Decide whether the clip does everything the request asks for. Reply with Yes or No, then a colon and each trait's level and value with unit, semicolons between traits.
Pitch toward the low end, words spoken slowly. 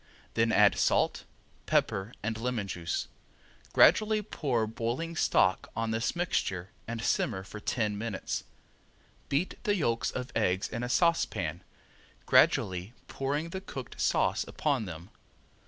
Yes: low, 115 Hz; slow, 130 wpm